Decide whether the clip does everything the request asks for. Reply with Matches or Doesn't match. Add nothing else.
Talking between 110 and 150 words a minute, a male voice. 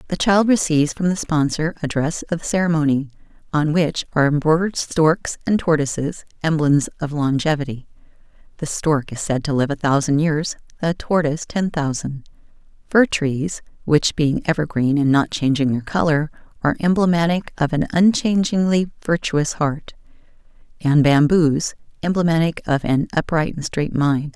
Doesn't match